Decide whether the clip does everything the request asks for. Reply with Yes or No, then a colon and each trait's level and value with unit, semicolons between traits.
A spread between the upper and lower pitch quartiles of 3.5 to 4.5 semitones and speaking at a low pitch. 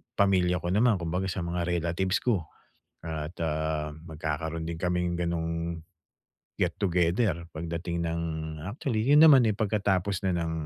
No: average, 2.9 semitones; very low, 85 Hz